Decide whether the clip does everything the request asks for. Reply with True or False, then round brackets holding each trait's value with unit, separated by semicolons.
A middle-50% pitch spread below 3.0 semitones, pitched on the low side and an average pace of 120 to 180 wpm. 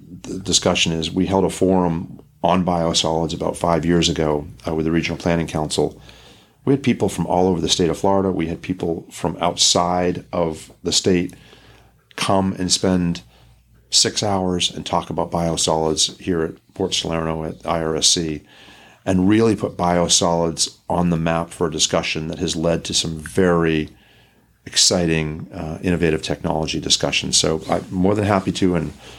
True (2.5 semitones; 85 Hz; 165 wpm)